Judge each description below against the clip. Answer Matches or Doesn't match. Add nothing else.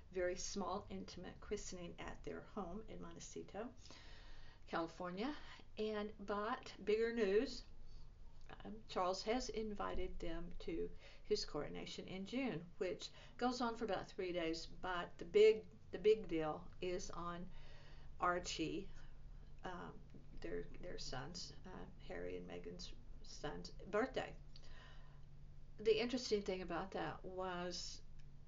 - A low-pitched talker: Doesn't match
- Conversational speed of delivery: Doesn't match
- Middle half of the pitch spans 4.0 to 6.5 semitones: Matches